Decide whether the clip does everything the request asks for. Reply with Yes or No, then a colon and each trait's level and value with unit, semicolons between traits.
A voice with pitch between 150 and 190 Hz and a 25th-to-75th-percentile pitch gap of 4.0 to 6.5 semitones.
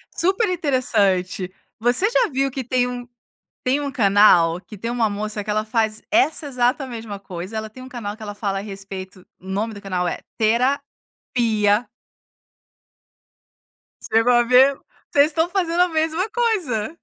No: high, 235 Hz; wide, 5.5 semitones